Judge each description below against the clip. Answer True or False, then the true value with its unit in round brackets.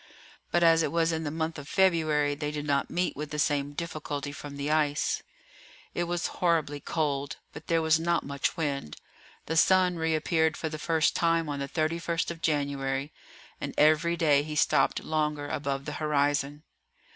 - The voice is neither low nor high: True (155 Hz)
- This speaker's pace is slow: False (180 wpm)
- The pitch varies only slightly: True (2.2 semitones)